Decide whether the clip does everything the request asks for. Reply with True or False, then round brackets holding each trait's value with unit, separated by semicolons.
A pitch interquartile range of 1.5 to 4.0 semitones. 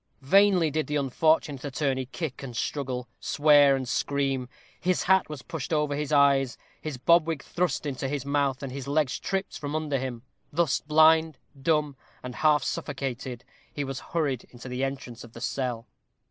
True (2.9 semitones)